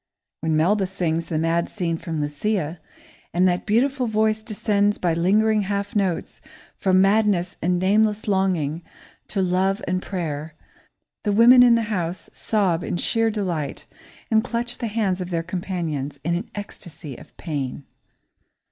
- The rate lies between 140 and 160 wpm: Yes, average, 150 wpm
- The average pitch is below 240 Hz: Yes, medium, 185 Hz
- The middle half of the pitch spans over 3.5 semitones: Yes, average, 4.1 semitones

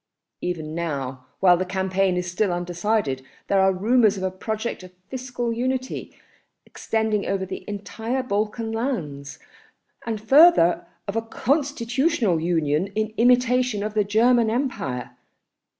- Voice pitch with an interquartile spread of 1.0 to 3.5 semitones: No, average, 5.0 semitones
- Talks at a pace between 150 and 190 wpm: No, slow, 135 wpm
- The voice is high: Yes, high, 210 Hz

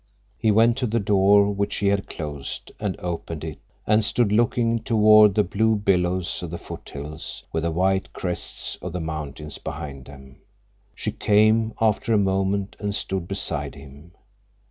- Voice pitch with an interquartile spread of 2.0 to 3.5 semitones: No, average, 4.7 semitones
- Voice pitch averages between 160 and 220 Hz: No, very low, 95 Hz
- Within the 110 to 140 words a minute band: No, average, 165 wpm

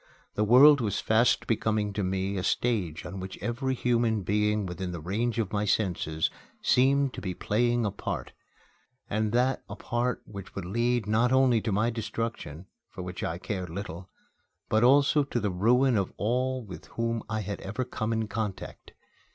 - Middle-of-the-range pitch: No, low, 110 Hz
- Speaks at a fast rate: No, average, 180 wpm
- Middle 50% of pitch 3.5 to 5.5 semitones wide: Yes, average, 3.8 semitones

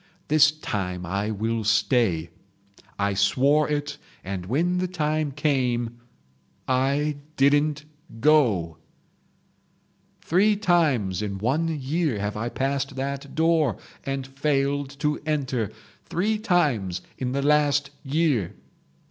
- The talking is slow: Yes, slow, 110 wpm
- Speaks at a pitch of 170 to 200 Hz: No, low, 135 Hz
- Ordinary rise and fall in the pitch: No, wide, 5.7 semitones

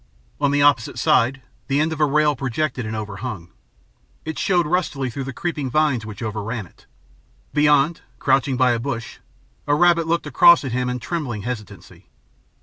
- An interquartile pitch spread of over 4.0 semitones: Yes, average, 4.4 semitones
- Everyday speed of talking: Yes, average, 170 wpm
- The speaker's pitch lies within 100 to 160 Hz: Yes, low, 135 Hz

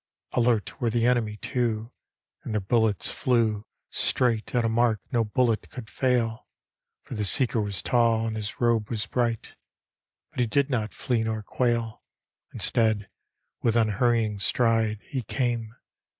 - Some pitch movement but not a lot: No, narrow, 1.9 semitones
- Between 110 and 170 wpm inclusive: Yes, average, 150 wpm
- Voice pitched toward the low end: Yes, low, 115 Hz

